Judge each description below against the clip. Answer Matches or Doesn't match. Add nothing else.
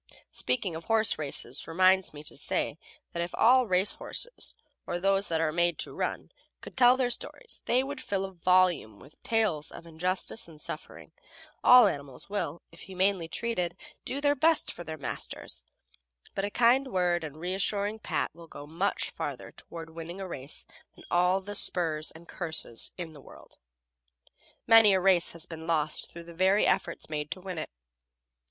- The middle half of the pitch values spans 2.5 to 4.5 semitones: Matches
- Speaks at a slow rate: Doesn't match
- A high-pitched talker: Doesn't match